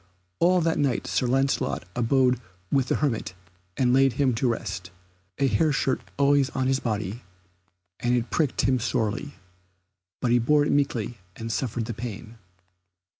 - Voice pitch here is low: Yes, low, 125 Hz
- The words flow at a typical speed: Yes, average, 160 wpm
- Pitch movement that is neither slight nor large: Yes, average, 3.0 semitones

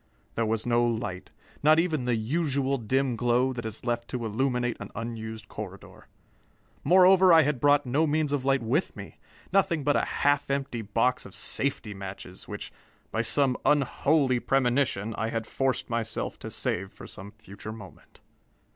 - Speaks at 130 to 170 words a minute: Yes, average, 165 wpm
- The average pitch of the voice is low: Yes, low, 125 Hz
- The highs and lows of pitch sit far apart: No, average, 4.1 semitones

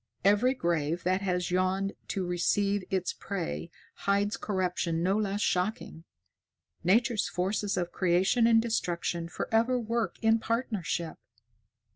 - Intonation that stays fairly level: No, average, 3.7 semitones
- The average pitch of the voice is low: No, high, 195 Hz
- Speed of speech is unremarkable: No, slow, 120 wpm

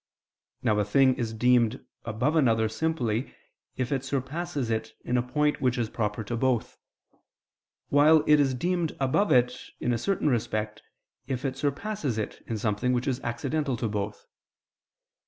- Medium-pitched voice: No, low, 125 Hz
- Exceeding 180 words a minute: No, average, 160 wpm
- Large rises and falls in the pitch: No, average, 4.1 semitones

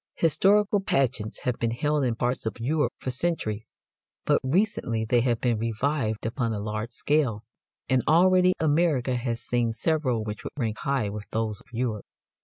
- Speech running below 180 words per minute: Yes, average, 170 wpm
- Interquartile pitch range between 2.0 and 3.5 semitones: No, average, 5.0 semitones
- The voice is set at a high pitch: No, low, 125 Hz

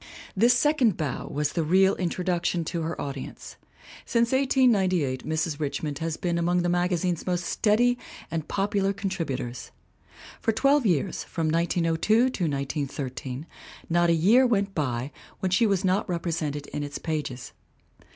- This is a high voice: No, medium, 175 Hz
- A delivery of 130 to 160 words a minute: Yes, average, 145 wpm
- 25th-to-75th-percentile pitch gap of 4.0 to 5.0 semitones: Yes, average, 4.6 semitones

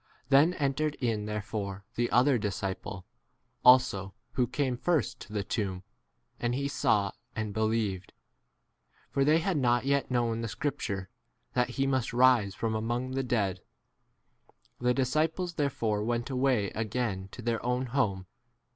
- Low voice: Yes, low, 120 Hz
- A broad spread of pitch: No, average, 4.3 semitones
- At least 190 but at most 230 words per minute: No, average, 155 wpm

